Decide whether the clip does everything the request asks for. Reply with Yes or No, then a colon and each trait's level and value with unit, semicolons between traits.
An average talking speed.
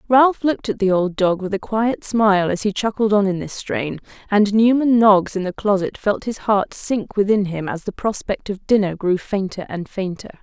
No: fast, 220 wpm